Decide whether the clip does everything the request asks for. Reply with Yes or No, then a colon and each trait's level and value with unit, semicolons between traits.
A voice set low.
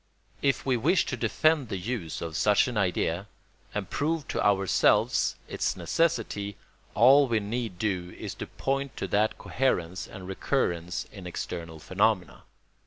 Yes: low, 105 Hz